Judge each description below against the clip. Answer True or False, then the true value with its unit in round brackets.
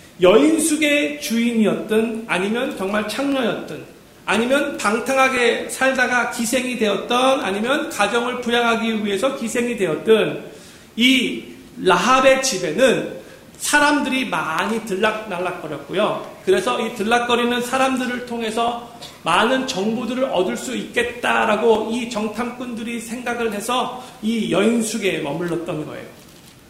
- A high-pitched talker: True (235 Hz)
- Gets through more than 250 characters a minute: True (285 characters per minute)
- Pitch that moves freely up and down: False (3.0 semitones)